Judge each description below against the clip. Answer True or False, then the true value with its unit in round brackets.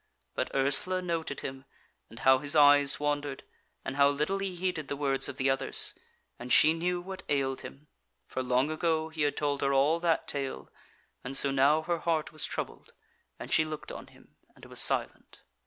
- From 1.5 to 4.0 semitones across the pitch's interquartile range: True (2.9 semitones)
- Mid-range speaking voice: True (145 Hz)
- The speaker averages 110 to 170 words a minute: False (190 wpm)